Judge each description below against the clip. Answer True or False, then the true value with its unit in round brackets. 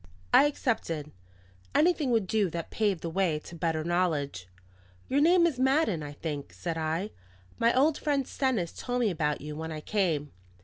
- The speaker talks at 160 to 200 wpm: True (175 wpm)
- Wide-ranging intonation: True (8.4 semitones)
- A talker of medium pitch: True (180 Hz)